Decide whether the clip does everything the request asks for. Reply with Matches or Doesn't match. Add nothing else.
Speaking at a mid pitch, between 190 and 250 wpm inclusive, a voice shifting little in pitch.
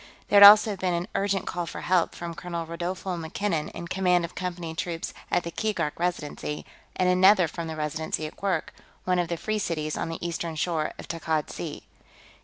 Matches